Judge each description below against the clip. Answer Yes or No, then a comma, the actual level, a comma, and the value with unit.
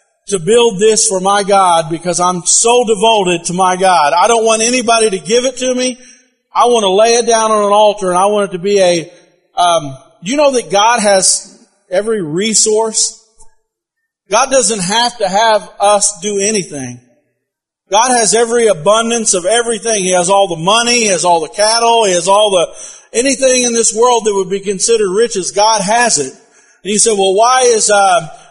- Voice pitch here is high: Yes, high, 215 Hz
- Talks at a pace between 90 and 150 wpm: No, average, 200 wpm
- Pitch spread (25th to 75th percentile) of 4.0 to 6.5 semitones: No, average, 3.5 semitones